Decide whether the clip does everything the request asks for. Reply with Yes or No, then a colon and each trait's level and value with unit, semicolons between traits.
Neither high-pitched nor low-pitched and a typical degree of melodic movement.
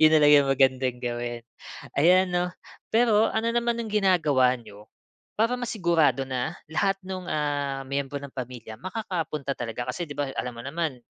No: medium, 145 Hz; wide, 6.3 semitones